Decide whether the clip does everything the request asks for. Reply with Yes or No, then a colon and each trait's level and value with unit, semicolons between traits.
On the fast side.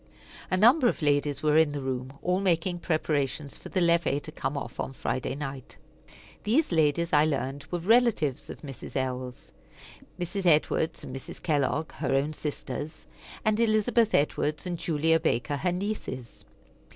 No: average, 160 wpm